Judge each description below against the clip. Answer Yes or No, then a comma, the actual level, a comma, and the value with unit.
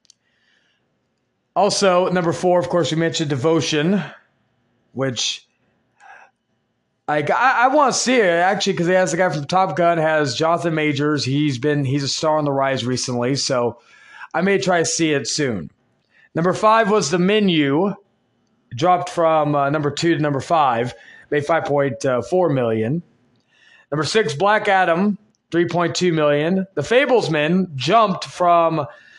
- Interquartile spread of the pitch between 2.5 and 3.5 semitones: No, average, 4.0 semitones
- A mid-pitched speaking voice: Yes, medium, 165 Hz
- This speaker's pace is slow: No, average, 155 wpm